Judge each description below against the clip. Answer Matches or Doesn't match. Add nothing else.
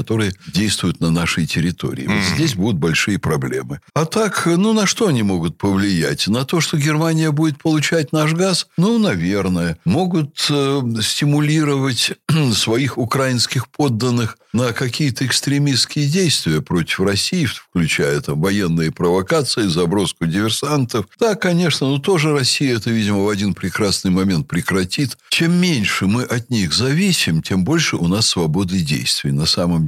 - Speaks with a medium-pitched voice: Doesn't match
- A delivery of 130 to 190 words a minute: Matches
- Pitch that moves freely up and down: Matches